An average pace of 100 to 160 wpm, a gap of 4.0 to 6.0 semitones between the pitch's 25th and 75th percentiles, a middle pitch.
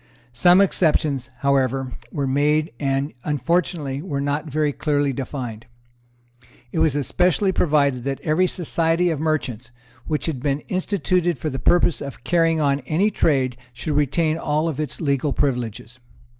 No: average, 145 wpm; average, 3.2 semitones; medium, 145 Hz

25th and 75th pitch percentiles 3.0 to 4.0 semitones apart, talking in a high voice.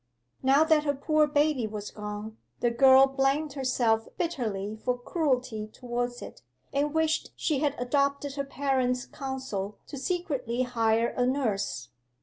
Yes: average, 3.5 semitones; very high, 260 Hz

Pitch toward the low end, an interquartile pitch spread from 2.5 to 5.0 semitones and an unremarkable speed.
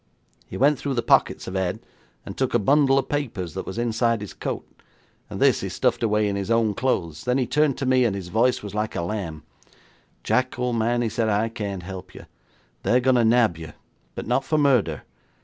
No: low, 115 Hz; average, 4.3 semitones; fast, 220 wpm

